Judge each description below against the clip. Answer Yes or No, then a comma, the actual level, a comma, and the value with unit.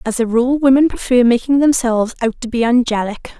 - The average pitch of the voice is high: Yes, high, 245 Hz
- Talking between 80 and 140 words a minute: No, average, 195 wpm